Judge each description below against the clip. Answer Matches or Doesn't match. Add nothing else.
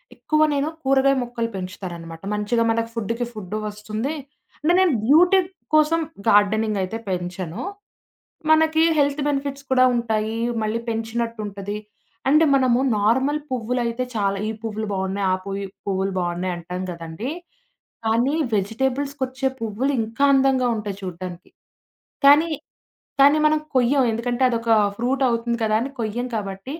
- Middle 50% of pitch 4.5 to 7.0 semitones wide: Matches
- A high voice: Matches